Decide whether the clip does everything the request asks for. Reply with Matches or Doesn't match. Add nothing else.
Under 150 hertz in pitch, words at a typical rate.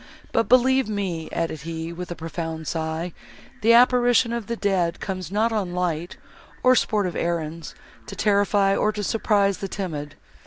Doesn't match